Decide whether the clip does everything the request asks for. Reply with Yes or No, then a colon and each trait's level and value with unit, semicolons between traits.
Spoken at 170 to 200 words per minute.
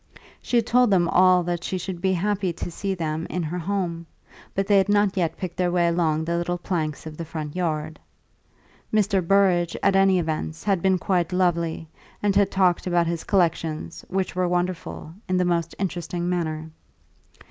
Yes: average, 190 wpm